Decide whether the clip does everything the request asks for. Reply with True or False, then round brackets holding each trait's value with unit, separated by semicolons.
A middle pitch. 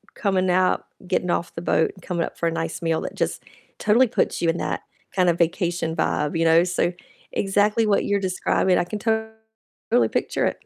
True (180 Hz)